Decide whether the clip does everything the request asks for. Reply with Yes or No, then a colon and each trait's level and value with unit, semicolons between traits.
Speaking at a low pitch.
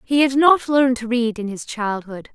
No: high, 245 Hz